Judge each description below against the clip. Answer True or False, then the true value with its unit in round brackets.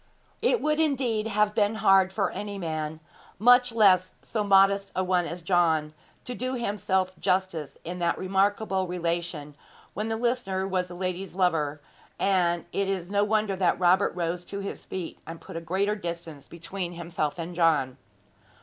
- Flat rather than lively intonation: False (3.1 semitones)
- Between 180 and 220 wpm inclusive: False (170 wpm)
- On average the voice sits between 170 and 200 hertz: True (185 Hz)